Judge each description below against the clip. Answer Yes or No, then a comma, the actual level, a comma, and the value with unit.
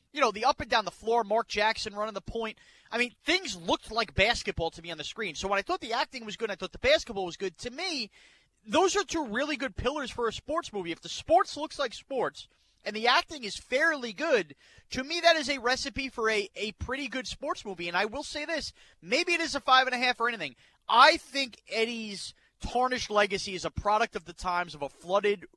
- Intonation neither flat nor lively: No, wide, 5.8 semitones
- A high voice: Yes, high, 235 Hz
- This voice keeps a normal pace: No, fast, 245 wpm